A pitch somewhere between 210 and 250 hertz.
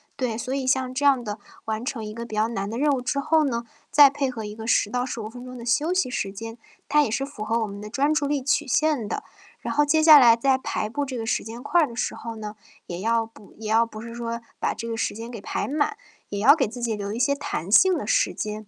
Yes: high, 235 Hz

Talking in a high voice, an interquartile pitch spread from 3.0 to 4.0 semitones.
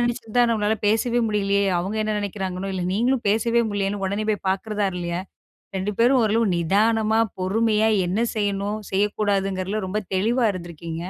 No: high, 205 Hz; narrow, 2.4 semitones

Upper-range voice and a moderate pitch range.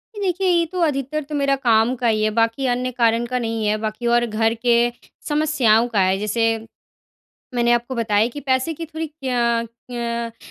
Yes: high, 240 Hz; average, 3.2 semitones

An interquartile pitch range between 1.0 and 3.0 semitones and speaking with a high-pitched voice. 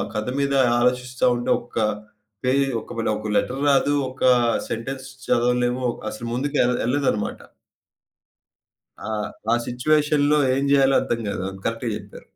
No: narrow, 2.6 semitones; low, 125 Hz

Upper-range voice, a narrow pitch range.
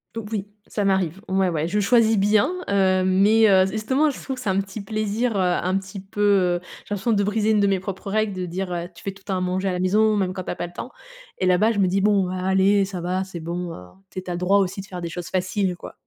Yes: high, 195 Hz; narrow, 2.1 semitones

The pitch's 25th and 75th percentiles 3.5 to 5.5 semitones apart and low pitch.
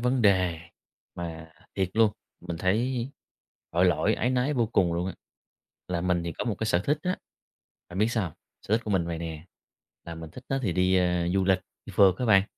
Yes: average, 4.7 semitones; very low, 95 Hz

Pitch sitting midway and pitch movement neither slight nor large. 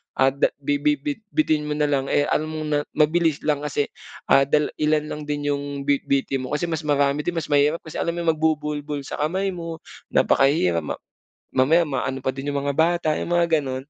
No: medium, 150 Hz; narrow, 2.1 semitones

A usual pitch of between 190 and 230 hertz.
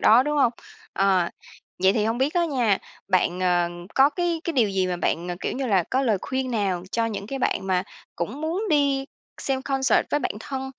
No: high, 240 Hz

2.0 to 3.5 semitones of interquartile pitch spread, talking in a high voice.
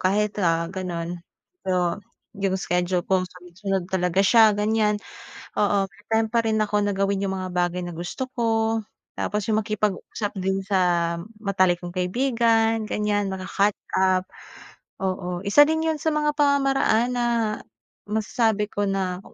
Yes: average, 3.1 semitones; high, 200 Hz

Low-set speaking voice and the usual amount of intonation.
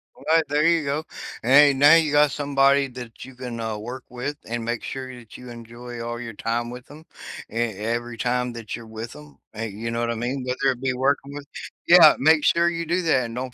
Yes: low, 125 Hz; average, 3.3 semitones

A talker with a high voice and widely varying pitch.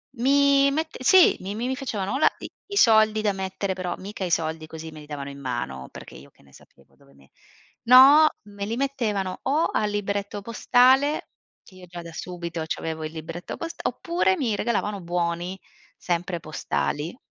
Yes: high, 195 Hz; wide, 7.0 semitones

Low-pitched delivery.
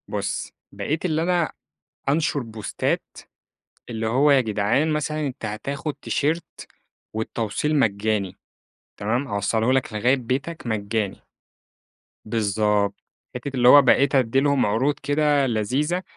Yes: low, 125 Hz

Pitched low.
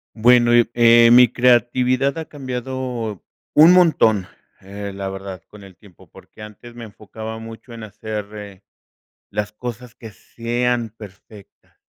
Yes: low, 115 Hz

